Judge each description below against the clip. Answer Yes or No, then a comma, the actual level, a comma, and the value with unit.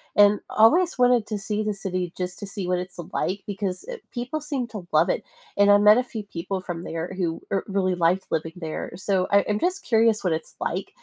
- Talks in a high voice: Yes, high, 200 Hz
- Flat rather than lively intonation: No, average, 3.2 semitones